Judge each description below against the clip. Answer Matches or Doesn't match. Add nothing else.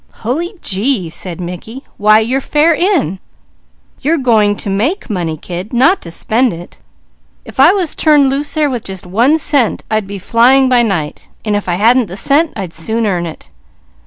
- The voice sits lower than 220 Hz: Doesn't match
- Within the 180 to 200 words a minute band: Matches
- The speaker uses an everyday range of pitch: Doesn't match